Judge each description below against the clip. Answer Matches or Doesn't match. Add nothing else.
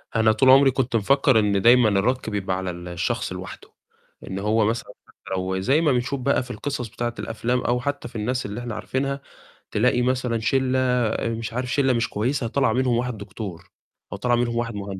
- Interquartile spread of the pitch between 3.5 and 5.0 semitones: Doesn't match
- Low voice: Matches